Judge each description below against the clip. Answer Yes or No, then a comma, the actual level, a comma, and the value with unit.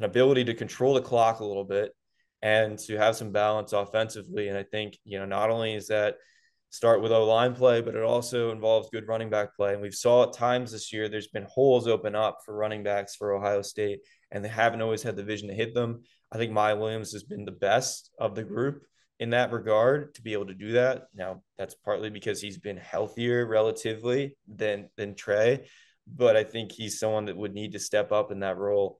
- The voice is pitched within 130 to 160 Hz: No, low, 110 Hz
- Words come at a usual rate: No, fast, 225 wpm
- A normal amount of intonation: No, narrow, 1.9 semitones